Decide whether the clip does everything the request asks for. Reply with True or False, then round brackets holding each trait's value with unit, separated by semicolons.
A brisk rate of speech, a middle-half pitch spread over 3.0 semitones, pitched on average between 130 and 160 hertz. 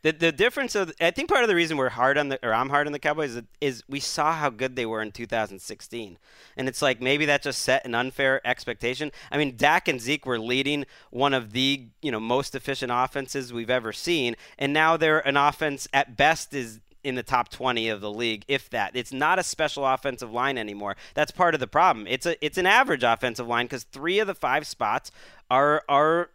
True (230 wpm; 3.4 semitones; 135 Hz)